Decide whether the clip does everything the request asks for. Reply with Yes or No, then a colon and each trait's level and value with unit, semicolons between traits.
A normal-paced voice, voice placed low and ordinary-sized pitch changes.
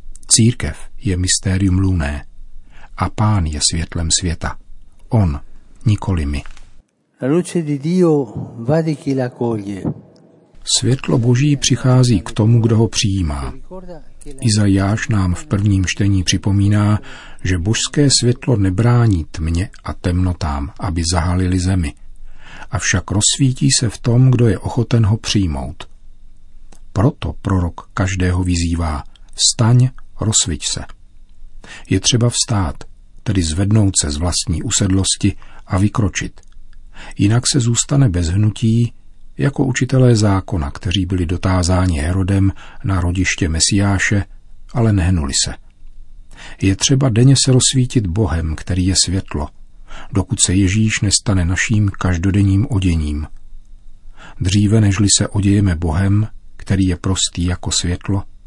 No: slow, 110 wpm; low, 100 Hz; average, 4.0 semitones